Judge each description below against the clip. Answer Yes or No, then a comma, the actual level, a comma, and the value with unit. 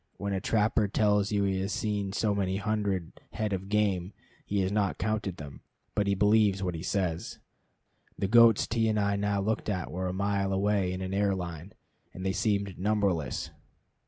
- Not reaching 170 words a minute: No, average, 190 wpm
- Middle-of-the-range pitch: No, low, 100 Hz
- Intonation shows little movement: Yes, narrow, 1.7 semitones